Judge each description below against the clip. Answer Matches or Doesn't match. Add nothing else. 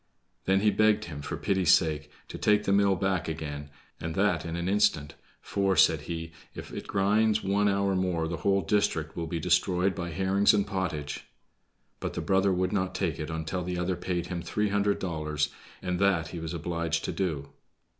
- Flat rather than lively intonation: Doesn't match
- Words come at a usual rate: Matches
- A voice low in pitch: Matches